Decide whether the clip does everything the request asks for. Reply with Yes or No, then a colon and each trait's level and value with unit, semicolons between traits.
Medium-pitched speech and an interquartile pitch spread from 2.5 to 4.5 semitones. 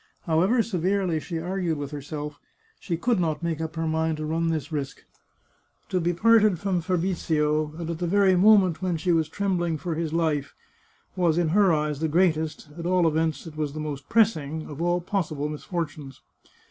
Yes: medium, 165 Hz; average, 2.8 semitones